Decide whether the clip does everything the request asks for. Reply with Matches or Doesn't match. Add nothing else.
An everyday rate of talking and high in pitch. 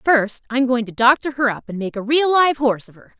Doesn't match